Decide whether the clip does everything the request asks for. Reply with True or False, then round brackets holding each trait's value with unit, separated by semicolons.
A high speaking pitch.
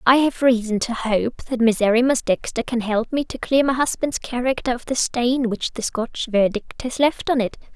True (240 Hz)